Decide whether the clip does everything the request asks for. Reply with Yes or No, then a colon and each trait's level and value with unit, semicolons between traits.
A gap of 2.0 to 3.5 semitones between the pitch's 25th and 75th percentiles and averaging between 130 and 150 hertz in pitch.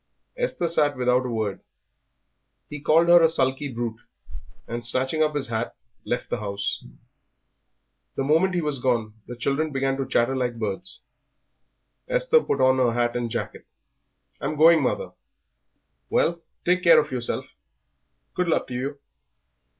No: average, 4.6 semitones; low, 135 Hz